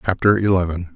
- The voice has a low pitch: Yes, very low, 95 Hz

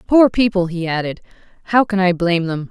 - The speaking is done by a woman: Yes, female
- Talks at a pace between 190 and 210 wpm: Yes, average, 200 wpm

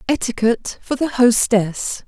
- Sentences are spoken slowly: Yes, slow, 115 wpm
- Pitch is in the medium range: No, high, 235 Hz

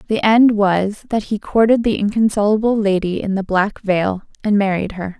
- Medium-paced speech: Yes, average, 185 wpm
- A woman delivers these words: Yes, female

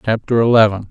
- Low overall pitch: Yes, low, 110 Hz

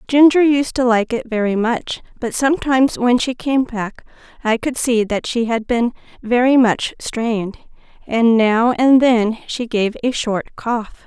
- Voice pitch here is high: Yes, high, 240 Hz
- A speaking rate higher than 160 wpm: Yes, average, 175 wpm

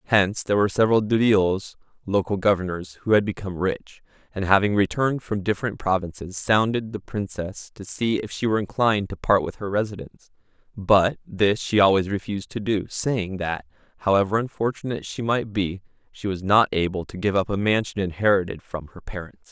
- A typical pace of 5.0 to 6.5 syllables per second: Yes, 5.6 syllables/s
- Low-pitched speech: Yes, low, 100 Hz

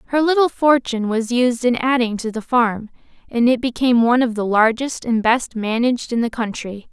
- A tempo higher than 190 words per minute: Yes, average, 200 wpm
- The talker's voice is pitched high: Yes, high, 240 Hz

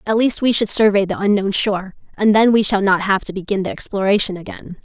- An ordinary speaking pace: No, fast, 235 wpm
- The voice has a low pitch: No, high, 200 Hz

